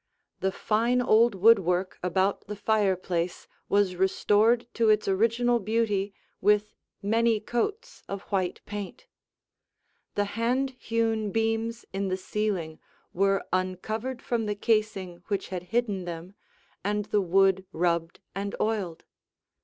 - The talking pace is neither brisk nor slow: No, slow, 125 wpm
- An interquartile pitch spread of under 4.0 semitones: Yes, average, 3.1 semitones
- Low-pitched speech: No, high, 205 Hz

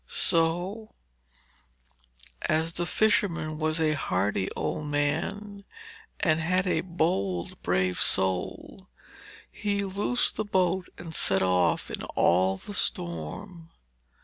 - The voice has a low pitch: No, medium, 160 Hz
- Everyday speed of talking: No, slow, 110 wpm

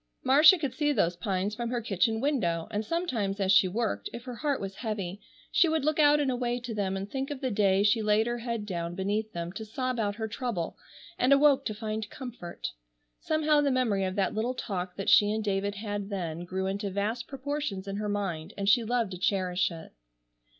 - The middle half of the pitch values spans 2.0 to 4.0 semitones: No, average, 4.5 semitones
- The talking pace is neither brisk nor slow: No, fast, 220 wpm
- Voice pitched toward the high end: Yes, high, 215 Hz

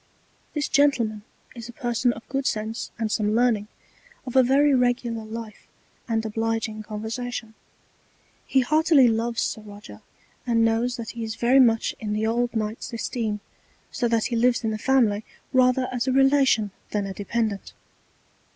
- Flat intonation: Yes, narrow, 2.3 semitones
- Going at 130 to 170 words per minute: Yes, average, 160 wpm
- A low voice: No, high, 230 Hz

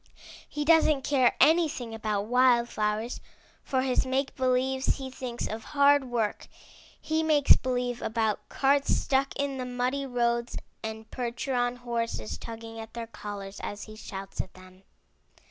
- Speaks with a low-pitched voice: No, high, 245 Hz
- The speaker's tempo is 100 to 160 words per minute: Yes, average, 145 wpm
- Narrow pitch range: No, average, 3.1 semitones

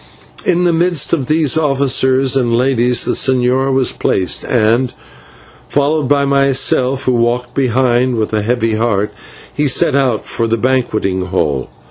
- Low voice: Yes, low, 130 Hz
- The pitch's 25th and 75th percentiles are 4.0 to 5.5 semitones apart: No, average, 2.7 semitones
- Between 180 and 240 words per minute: No, average, 150 wpm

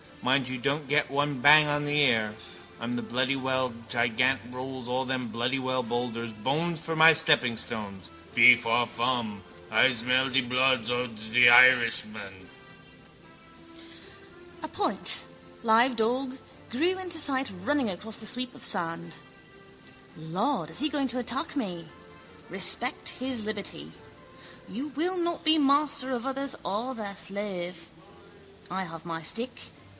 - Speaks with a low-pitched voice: No, medium, 150 Hz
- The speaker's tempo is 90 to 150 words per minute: Yes, average, 140 wpm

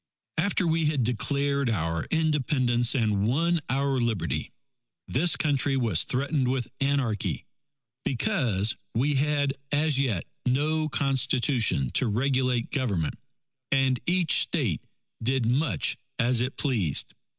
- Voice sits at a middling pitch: No, low, 130 Hz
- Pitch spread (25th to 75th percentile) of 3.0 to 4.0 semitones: Yes, average, 3.5 semitones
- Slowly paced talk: Yes, slow, 115 wpm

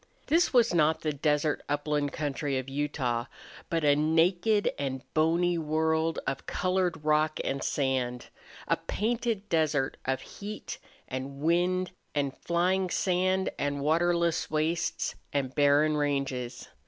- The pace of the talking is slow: Yes, slow, 130 wpm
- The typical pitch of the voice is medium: Yes, medium, 155 Hz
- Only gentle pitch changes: No, average, 3.6 semitones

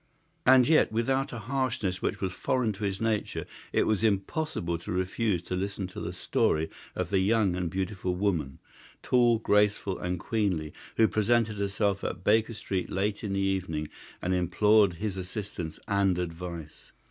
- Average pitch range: Yes, average, 3.3 semitones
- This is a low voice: Yes, low, 100 Hz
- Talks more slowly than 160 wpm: No, average, 165 wpm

